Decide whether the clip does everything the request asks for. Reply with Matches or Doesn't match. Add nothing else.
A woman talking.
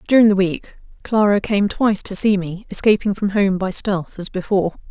Matches